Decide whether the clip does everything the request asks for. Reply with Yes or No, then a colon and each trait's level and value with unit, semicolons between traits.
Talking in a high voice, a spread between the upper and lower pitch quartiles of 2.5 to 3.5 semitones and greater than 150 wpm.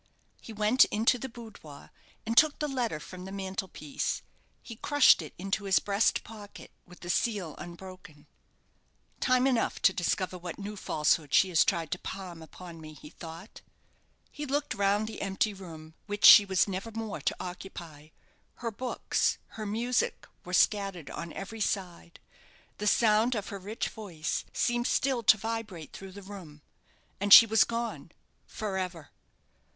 No: high, 200 Hz; average, 4.2 semitones; average, 165 wpm